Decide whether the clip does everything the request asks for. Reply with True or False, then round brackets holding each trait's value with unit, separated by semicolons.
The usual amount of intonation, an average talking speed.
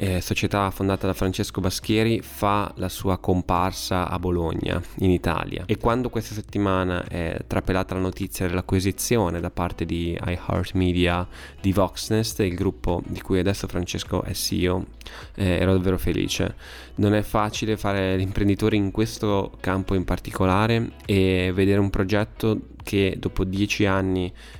False (2.2 semitones; 145 wpm)